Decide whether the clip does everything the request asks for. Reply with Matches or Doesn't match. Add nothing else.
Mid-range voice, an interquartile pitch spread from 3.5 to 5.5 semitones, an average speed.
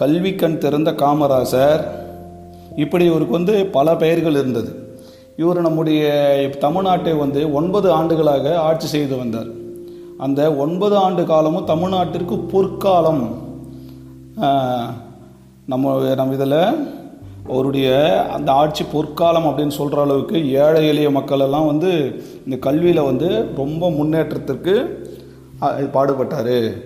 Matches